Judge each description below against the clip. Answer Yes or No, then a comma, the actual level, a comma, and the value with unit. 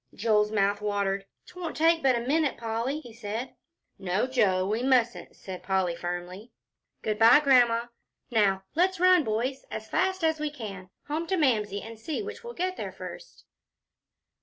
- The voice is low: No, high, 235 Hz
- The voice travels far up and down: Yes, wide, 6.9 semitones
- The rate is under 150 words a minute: No, average, 165 wpm